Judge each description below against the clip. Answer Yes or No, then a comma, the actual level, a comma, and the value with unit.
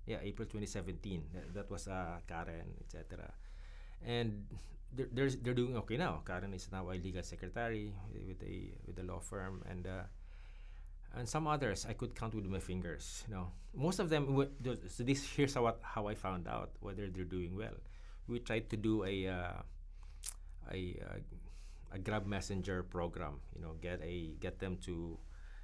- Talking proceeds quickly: No, average, 180 wpm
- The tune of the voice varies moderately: Yes, average, 4.1 semitones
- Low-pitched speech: Yes, very low, 95 Hz